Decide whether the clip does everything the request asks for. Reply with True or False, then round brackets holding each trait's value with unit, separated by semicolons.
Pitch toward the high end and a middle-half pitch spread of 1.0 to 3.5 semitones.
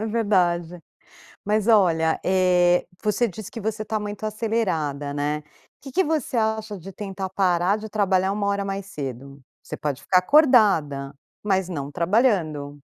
False (195 Hz; 4.8 semitones)